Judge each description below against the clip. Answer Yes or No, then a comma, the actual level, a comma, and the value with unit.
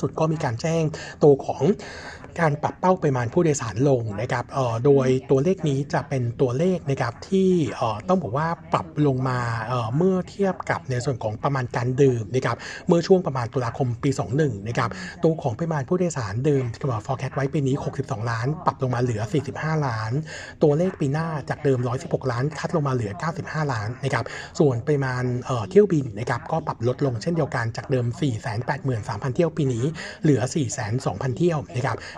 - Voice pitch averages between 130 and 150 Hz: Yes, medium, 140 Hz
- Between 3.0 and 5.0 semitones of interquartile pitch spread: Yes, average, 3.8 semitones